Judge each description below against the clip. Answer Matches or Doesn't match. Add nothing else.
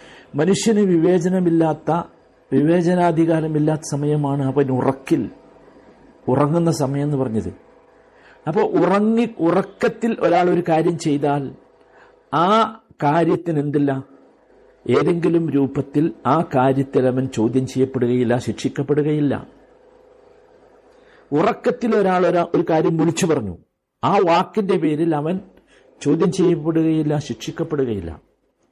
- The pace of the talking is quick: Doesn't match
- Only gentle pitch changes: Doesn't match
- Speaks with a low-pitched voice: Doesn't match